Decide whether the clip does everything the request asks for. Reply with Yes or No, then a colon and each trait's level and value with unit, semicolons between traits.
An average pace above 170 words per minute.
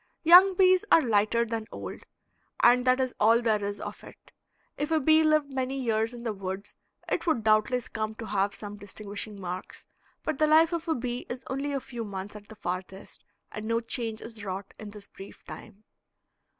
Yes: average, 200 wpm